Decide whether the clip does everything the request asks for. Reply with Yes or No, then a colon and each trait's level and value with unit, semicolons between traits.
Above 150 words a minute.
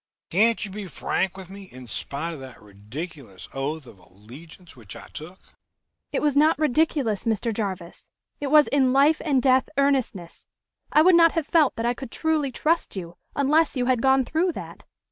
Yes: average, 185 wpm